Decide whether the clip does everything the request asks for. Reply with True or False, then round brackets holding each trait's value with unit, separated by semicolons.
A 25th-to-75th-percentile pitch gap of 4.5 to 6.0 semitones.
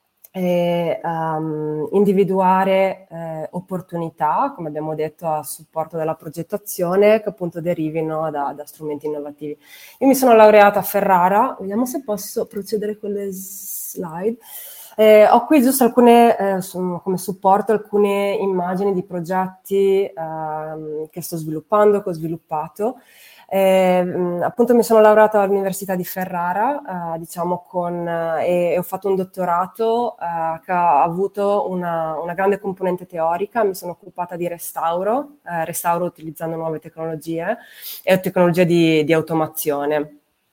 False (3.6 semitones)